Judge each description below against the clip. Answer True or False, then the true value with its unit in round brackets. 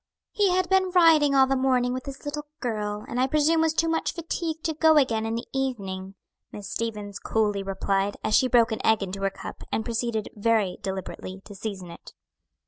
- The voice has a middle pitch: False (235 Hz)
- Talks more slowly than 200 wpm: False (205 wpm)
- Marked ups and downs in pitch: True (6.6 semitones)